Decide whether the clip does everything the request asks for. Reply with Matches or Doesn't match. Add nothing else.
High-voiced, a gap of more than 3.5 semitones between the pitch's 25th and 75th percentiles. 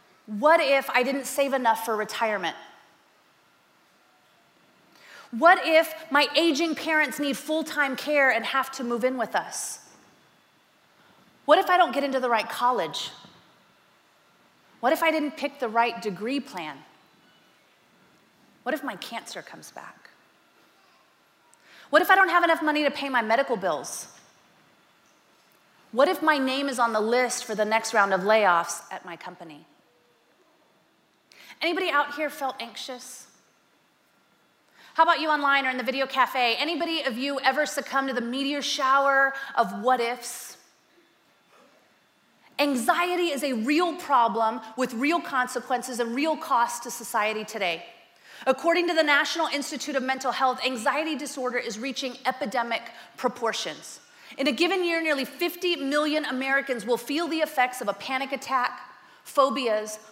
Matches